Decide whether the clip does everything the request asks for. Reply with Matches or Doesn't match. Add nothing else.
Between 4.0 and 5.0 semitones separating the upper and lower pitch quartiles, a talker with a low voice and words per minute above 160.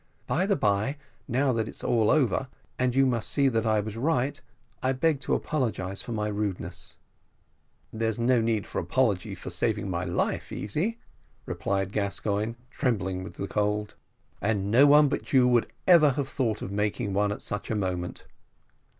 Matches